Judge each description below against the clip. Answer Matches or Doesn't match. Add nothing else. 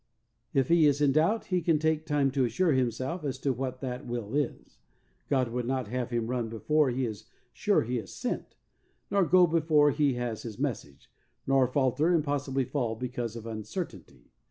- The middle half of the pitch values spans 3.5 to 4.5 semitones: Matches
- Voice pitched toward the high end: Doesn't match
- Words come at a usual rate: Matches